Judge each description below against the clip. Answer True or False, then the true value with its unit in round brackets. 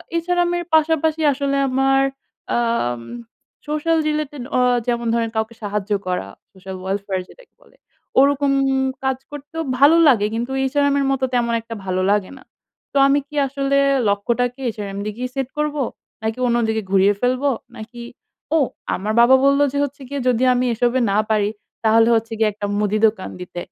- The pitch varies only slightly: False (4.8 semitones)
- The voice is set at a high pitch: True (245 Hz)